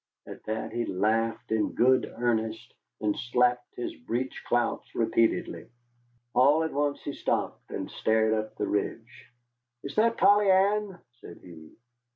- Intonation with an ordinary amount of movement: Yes, average, 4.4 semitones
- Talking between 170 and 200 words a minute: No, average, 145 wpm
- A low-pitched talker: Yes, low, 120 Hz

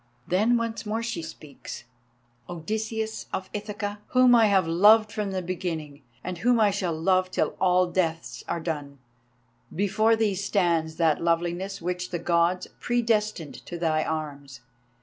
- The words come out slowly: No, average, 150 wpm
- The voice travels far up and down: No, average, 4.2 semitones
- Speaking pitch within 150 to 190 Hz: Yes, medium, 185 Hz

